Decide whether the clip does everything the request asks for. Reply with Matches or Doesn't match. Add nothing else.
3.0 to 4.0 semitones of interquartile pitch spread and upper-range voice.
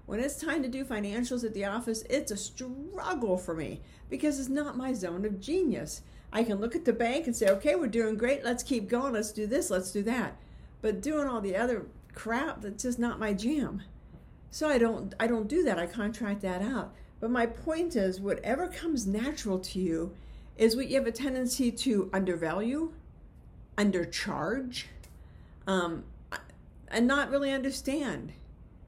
Doesn't match